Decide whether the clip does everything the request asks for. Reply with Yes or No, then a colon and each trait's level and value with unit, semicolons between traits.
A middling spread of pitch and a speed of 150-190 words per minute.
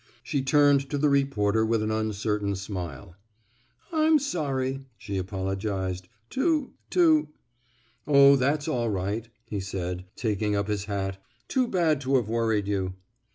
No: wide, 5.8 semitones; average, 155 wpm